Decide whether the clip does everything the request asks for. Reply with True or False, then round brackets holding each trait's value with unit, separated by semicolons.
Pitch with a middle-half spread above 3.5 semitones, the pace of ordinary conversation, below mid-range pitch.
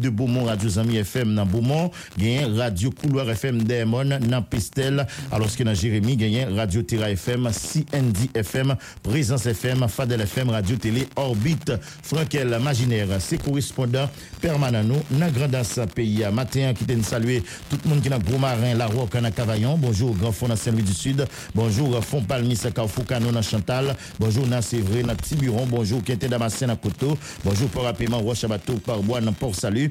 False (3.0 semitones; 175 wpm; 120 Hz)